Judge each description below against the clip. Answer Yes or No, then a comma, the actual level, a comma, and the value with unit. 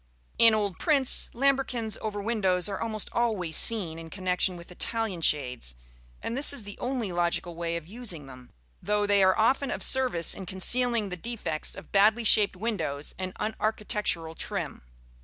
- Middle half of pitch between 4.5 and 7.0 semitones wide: Yes, average, 4.8 semitones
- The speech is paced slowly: No, average, 165 wpm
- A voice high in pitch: Yes, high, 205 Hz